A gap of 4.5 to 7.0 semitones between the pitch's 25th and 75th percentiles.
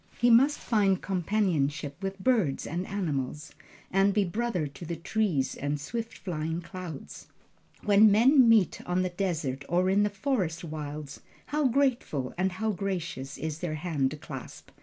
Yes: average, 5.2 semitones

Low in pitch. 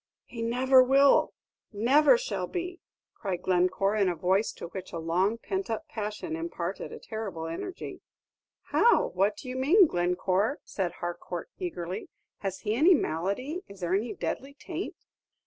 No: high, 210 Hz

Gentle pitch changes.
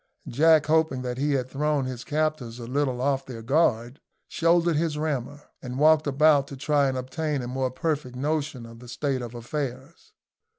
No: average, 3.2 semitones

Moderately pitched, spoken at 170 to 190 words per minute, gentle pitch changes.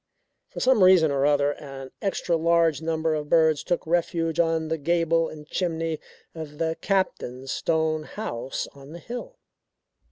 No: medium, 160 Hz; average, 155 wpm; narrow, 2.1 semitones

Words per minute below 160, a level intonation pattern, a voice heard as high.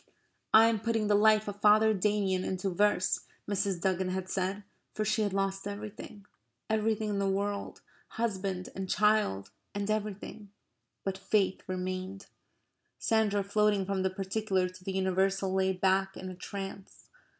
Yes: average, 150 wpm; narrow, 1.9 semitones; high, 195 Hz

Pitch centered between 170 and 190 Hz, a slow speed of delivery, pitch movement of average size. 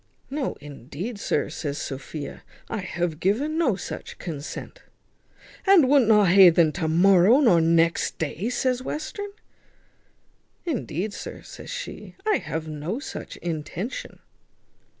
No: medium, 185 Hz; slow, 130 wpm; wide, 8.1 semitones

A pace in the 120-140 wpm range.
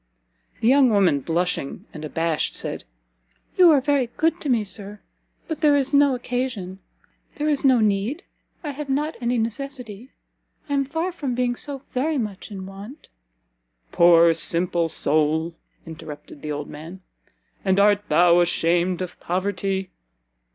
No: average, 150 wpm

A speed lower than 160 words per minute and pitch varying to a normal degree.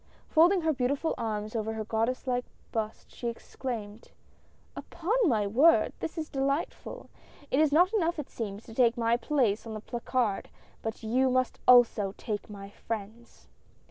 No: average, 165 wpm; average, 4.5 semitones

